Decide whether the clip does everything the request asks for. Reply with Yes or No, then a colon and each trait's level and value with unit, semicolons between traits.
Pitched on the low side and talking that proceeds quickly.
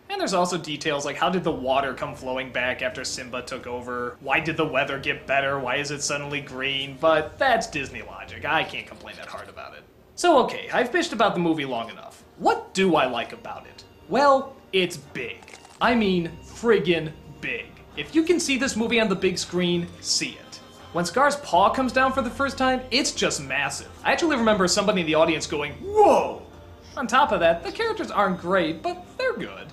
No: medium, 180 Hz; fast, 210 wpm